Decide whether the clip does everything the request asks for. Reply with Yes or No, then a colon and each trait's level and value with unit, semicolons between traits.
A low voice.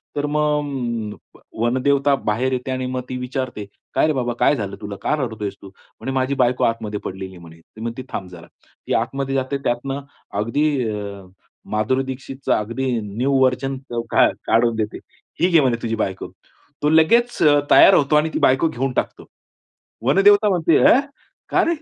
Yes: low, 130 Hz